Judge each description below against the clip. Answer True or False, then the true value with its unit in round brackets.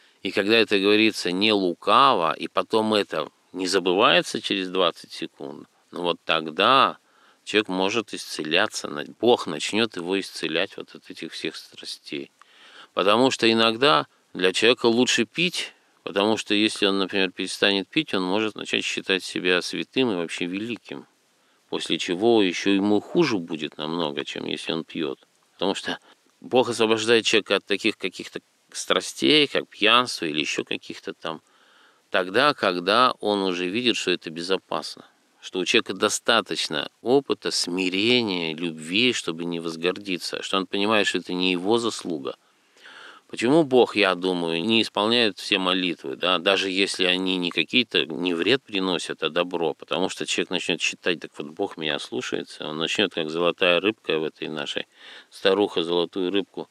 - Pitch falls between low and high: False (100 Hz)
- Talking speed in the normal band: True (150 wpm)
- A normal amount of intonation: True (3.4 semitones)